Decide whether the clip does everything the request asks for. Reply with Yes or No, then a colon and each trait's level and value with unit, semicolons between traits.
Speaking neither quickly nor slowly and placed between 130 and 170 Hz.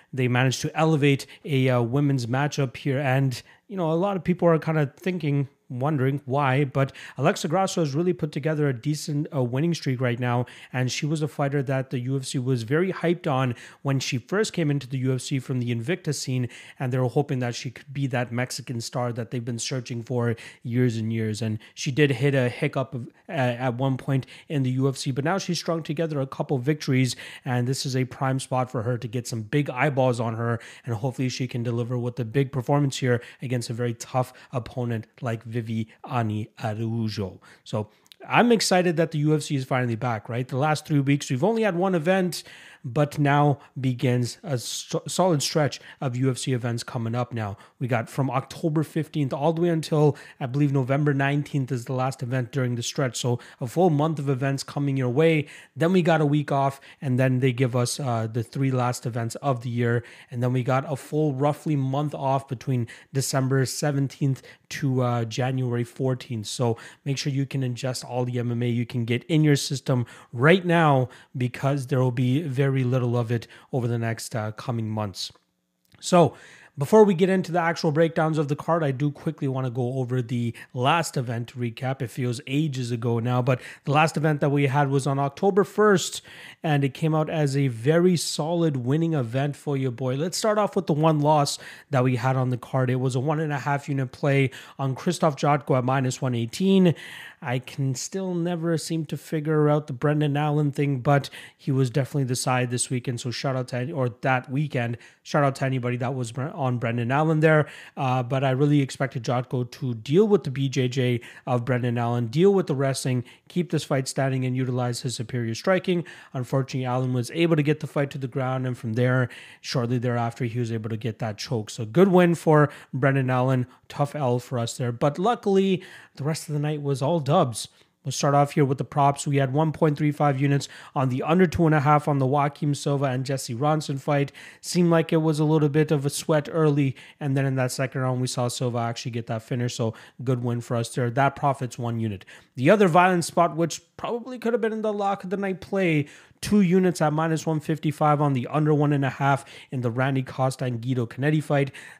No: fast, 215 wpm; low, 135 Hz